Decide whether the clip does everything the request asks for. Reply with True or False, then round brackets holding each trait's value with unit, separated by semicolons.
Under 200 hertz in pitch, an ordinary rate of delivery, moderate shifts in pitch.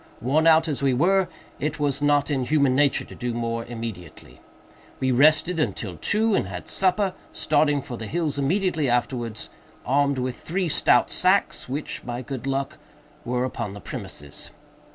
True (140 Hz; 165 wpm; 4.2 semitones)